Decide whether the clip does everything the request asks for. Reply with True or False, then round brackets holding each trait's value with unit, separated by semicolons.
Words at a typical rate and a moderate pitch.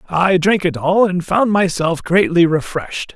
True (170 wpm; 175 Hz)